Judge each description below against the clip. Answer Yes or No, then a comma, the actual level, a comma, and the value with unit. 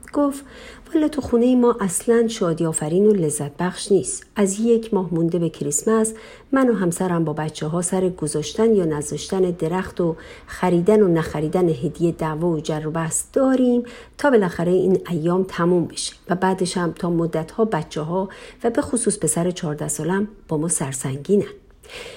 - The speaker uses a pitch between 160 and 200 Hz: Yes, medium, 185 Hz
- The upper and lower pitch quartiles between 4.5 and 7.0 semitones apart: Yes, wide, 5.5 semitones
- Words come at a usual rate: No, fast, 175 wpm